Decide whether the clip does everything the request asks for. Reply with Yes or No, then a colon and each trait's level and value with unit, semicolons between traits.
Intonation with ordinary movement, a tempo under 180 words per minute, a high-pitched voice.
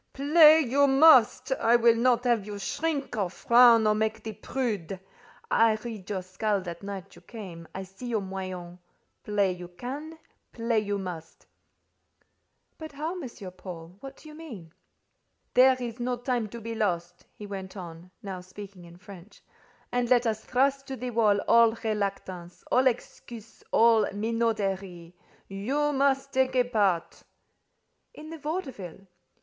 Yes: average, 4.8 semitones; average, 155 wpm; high, 220 Hz